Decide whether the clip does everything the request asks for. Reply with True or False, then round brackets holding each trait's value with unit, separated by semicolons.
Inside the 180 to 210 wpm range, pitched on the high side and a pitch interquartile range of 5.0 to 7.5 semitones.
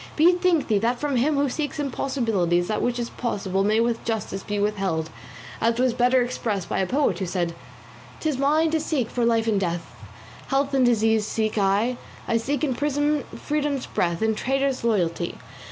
True (185 wpm; 235 Hz; 5.3 semitones)